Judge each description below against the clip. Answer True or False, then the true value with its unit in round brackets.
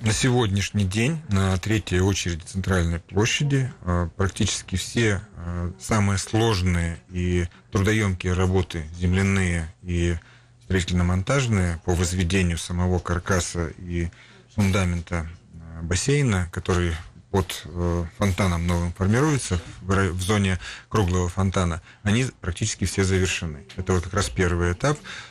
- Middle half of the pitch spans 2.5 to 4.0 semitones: True (3.0 semitones)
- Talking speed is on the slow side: True (105 wpm)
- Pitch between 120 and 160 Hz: False (95 Hz)